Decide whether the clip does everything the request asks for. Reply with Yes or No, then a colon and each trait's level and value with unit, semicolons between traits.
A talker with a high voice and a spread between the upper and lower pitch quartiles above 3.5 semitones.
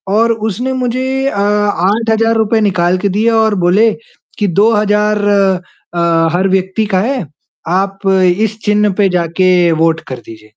No: high, 205 Hz; average, 3.2 semitones